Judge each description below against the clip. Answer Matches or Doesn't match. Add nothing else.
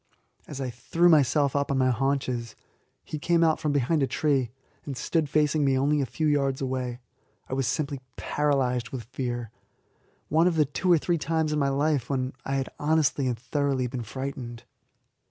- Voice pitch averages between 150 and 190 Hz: Doesn't match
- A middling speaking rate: Matches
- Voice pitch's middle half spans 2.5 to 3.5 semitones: Matches